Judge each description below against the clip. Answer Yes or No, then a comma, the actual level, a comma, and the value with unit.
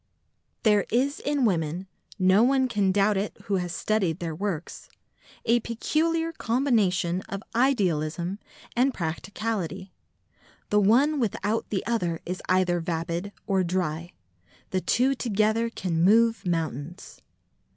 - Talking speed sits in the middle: No, slow, 120 wpm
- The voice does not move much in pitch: No, average, 4.8 semitones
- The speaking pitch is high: Yes, high, 200 Hz